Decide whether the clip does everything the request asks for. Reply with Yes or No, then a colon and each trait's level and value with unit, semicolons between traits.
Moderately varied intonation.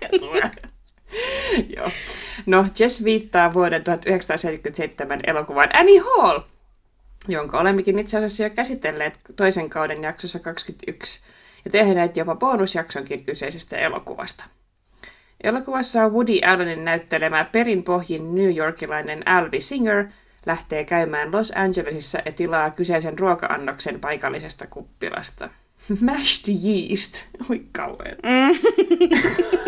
No: wide, 5.9 semitones